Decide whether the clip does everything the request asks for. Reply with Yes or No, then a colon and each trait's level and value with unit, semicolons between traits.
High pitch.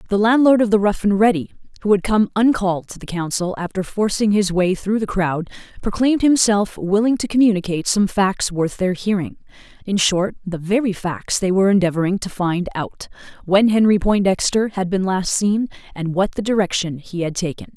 Yes: high, 195 Hz